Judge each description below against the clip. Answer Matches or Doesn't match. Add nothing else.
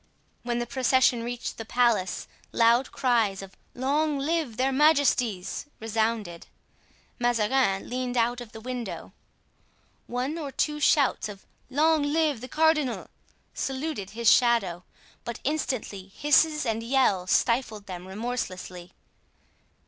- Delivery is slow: Matches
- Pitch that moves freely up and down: Doesn't match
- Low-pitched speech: Doesn't match